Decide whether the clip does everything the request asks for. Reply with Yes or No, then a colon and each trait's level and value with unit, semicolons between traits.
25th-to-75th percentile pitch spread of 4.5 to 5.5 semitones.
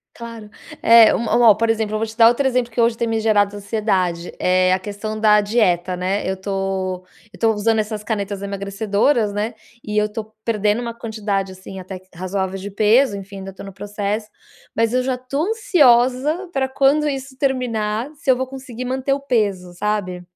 No: average, 3.4 semitones